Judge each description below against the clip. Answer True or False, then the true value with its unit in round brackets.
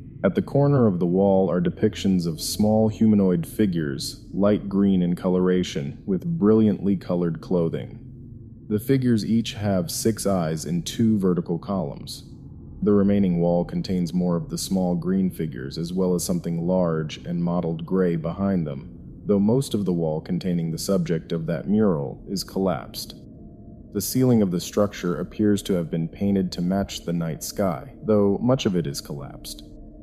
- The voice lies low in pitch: True (95 Hz)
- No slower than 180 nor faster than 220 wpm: False (170 wpm)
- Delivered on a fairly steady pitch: False (3.2 semitones)